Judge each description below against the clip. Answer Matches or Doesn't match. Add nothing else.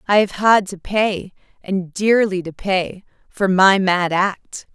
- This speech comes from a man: Doesn't match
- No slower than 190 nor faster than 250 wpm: Doesn't match